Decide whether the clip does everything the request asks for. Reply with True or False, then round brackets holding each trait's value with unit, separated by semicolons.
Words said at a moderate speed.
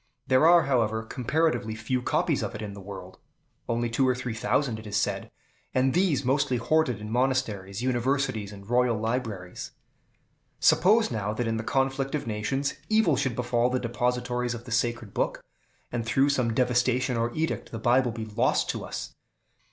True (175 wpm)